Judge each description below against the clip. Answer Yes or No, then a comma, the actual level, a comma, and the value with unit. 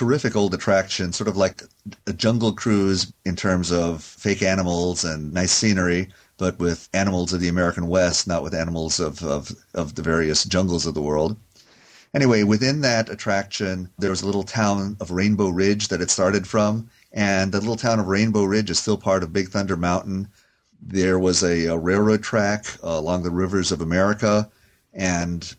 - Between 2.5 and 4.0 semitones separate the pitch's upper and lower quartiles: Yes, average, 2.9 semitones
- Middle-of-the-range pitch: No, very low, 95 Hz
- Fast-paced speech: No, average, 185 wpm